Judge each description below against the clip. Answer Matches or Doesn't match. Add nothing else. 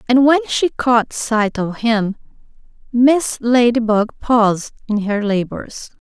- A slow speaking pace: Matches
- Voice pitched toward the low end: Doesn't match